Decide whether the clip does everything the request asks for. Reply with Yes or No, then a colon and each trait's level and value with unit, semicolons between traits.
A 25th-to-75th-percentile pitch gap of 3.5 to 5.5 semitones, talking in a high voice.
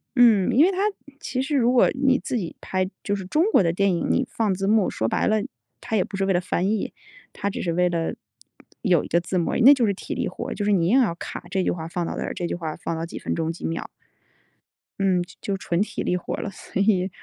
Yes: average, 4.1 semitones; high, 195 Hz